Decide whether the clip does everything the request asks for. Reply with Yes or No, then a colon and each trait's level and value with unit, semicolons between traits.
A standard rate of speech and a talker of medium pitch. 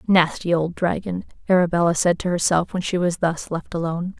Yes: average, 185 wpm; medium, 175 Hz